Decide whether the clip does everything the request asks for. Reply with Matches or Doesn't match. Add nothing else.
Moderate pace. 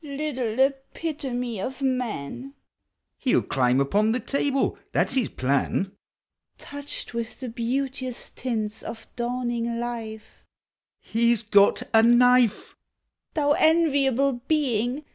Doesn't match